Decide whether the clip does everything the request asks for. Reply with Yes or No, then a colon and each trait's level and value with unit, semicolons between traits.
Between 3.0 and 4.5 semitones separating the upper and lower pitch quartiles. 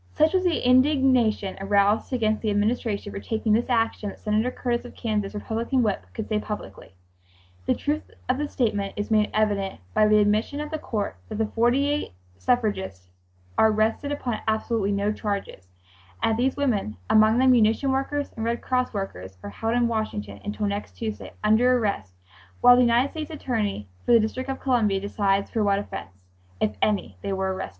Yes: average, 3.5 semitones